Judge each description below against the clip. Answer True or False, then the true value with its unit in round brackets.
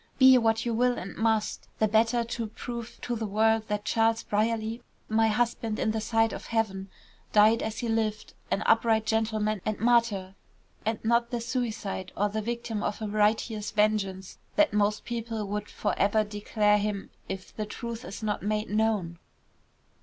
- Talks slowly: False (175 wpm)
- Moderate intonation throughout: False (1.5 semitones)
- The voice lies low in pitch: False (220 Hz)